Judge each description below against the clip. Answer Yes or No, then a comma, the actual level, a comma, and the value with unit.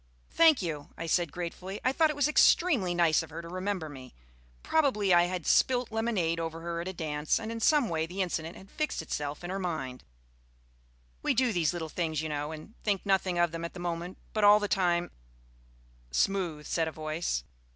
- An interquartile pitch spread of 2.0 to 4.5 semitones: Yes, average, 4.2 semitones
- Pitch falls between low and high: Yes, medium, 175 Hz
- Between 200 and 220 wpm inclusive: Yes, fast, 205 wpm